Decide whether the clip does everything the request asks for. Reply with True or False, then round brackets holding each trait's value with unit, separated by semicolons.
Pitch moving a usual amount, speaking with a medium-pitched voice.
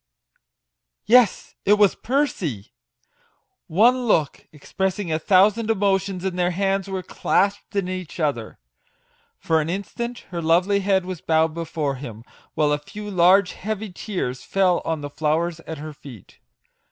True (4.1 semitones; 180 Hz)